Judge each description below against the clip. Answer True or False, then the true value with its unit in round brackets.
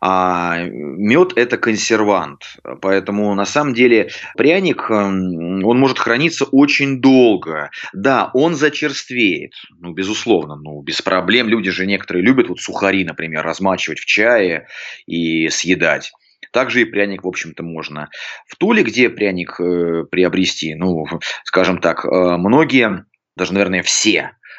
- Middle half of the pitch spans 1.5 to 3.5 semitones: False (4.4 semitones)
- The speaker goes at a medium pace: True (130 wpm)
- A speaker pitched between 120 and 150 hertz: False (95 Hz)